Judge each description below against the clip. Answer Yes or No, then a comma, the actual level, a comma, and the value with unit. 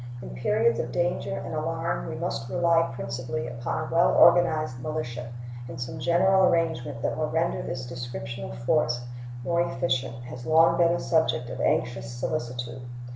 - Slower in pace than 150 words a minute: No, average, 165 wpm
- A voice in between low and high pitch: No, low, 125 Hz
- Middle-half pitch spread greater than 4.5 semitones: Yes, average, 5.2 semitones